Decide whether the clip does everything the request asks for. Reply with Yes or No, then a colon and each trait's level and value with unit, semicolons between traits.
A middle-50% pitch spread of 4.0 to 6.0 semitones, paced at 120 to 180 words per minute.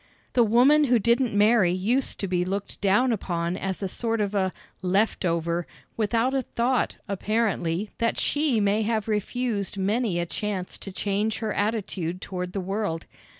No: average, 3.6 semitones; average, 160 wpm